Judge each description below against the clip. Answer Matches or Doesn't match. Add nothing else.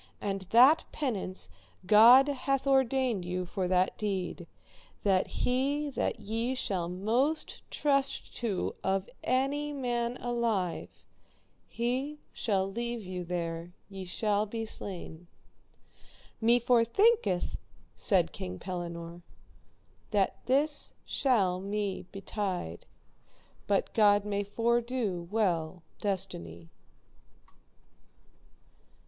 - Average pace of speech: Doesn't match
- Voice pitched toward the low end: Doesn't match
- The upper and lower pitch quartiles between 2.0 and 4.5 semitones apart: Doesn't match